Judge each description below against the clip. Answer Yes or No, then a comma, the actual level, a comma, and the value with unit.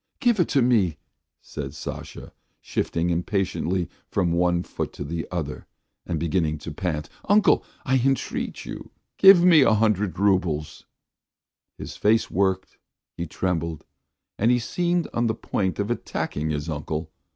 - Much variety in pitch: Yes, wide, 6.4 semitones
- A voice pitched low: Yes, very low, 95 Hz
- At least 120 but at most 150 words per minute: Yes, average, 140 wpm